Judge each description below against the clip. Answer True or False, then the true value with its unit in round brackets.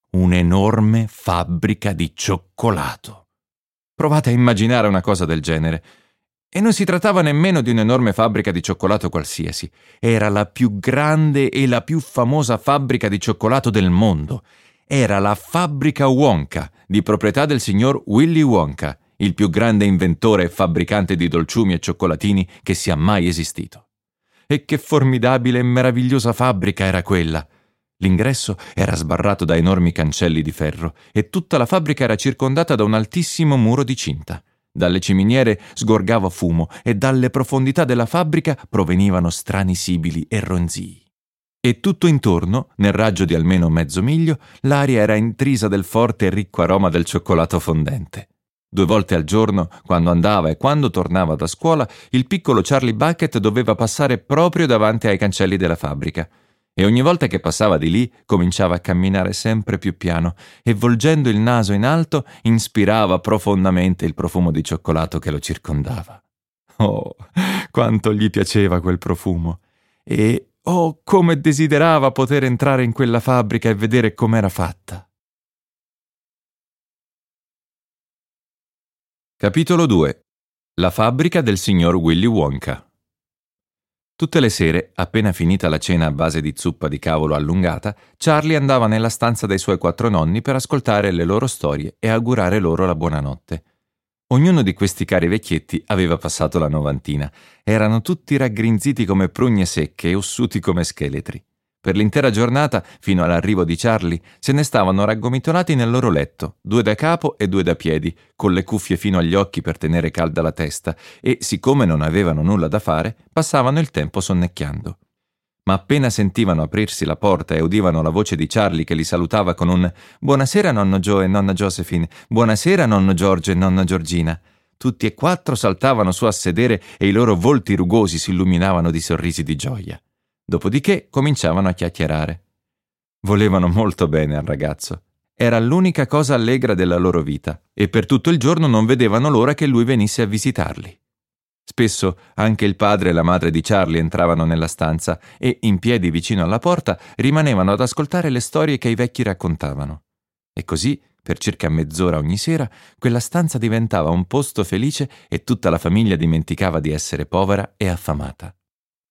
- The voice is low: True (105 Hz)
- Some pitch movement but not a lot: False (6.2 semitones)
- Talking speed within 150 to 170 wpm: True (160 wpm)